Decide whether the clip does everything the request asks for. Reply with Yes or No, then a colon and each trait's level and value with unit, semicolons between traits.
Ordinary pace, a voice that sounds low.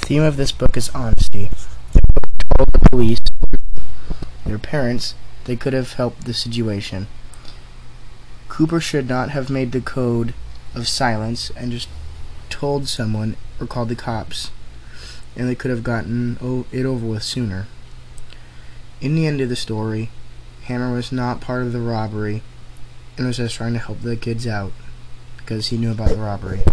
Yes: average, 165 wpm; low, 120 Hz